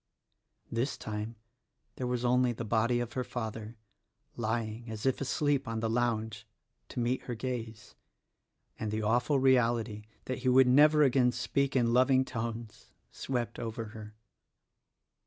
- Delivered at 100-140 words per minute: No, average, 155 wpm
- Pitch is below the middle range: Yes, low, 120 Hz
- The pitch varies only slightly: Yes, narrow, 2.3 semitones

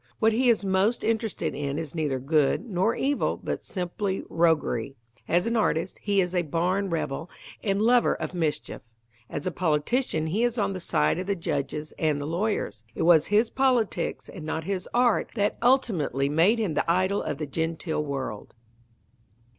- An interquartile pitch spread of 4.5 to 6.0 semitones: Yes, wide, 5.6 semitones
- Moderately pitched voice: Yes, medium, 180 Hz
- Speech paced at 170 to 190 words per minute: Yes, average, 180 wpm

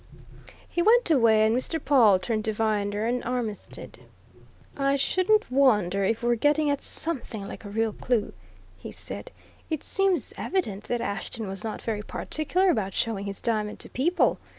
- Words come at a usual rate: Yes, average, 165 wpm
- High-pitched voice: Yes, high, 230 Hz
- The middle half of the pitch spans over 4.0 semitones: Yes, wide, 5.6 semitones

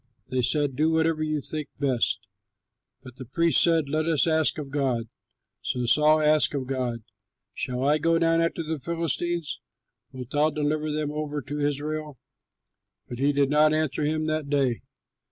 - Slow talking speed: No, average, 170 wpm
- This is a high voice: No, medium, 150 Hz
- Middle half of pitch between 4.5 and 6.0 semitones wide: No, narrow, 2.4 semitones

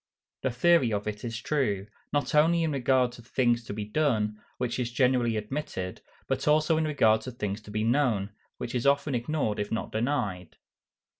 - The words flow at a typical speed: Yes, average, 195 wpm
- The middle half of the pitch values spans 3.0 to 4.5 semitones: No, average, 4.9 semitones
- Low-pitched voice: Yes, low, 120 Hz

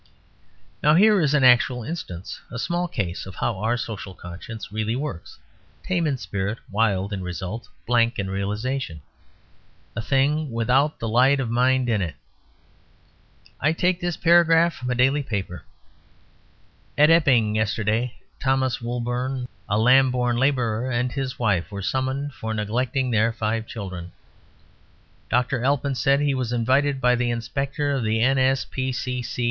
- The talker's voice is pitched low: Yes, low, 125 Hz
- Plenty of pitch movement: No, average, 3.8 semitones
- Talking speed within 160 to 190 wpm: No, average, 145 wpm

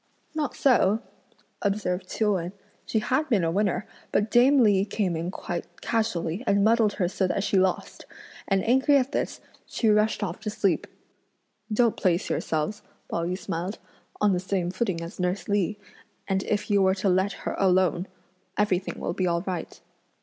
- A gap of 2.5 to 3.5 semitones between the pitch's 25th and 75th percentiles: Yes, average, 2.8 semitones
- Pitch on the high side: Yes, high, 195 Hz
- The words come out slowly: No, average, 175 wpm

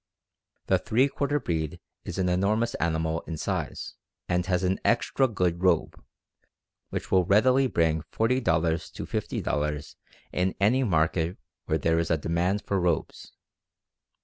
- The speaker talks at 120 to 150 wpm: Yes, average, 140 wpm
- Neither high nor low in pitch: No, very low, 90 Hz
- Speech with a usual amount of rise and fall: Yes, average, 4.6 semitones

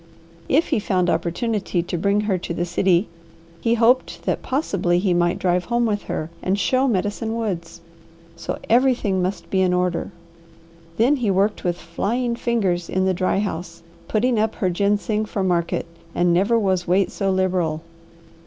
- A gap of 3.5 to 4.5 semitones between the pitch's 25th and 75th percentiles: Yes, average, 3.8 semitones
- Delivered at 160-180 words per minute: Yes, average, 170 wpm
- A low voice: No, high, 190 Hz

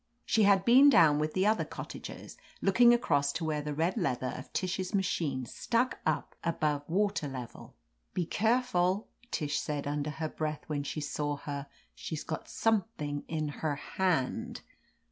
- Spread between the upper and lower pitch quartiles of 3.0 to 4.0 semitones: No, average, 4.9 semitones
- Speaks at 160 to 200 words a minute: Yes, average, 165 wpm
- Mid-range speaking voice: Yes, medium, 160 Hz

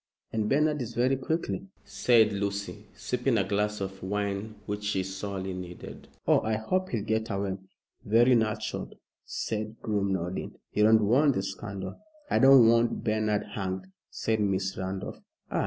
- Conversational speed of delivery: Yes, average, 155 wpm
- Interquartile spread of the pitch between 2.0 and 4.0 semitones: Yes, average, 2.8 semitones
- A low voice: Yes, low, 105 Hz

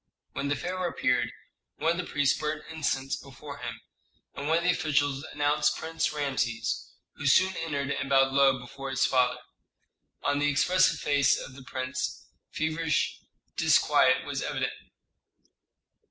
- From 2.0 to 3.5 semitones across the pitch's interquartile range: Yes, narrow, 2.6 semitones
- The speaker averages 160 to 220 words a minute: No, average, 150 wpm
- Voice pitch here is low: No, medium, 145 Hz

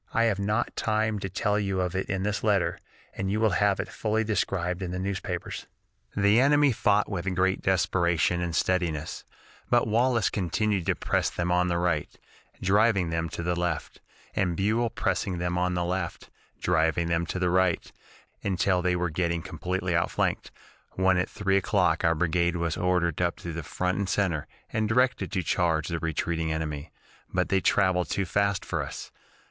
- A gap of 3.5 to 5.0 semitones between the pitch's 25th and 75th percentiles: No, average, 2.7 semitones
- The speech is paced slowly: No, average, 185 wpm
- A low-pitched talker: Yes, very low, 90 Hz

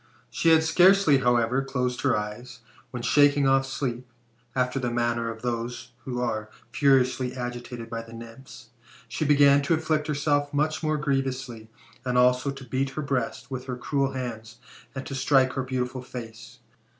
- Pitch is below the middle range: Yes, low, 130 Hz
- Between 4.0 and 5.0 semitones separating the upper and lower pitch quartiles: No, narrow, 2.4 semitones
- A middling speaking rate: Yes, average, 165 wpm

